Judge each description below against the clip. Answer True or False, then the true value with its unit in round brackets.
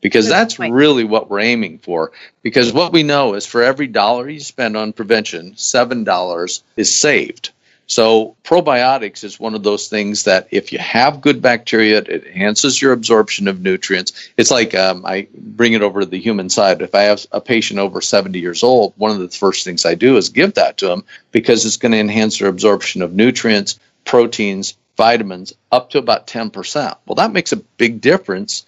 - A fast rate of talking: False (195 wpm)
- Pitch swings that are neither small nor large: True (3.2 semitones)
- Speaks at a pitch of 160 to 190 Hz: False (110 Hz)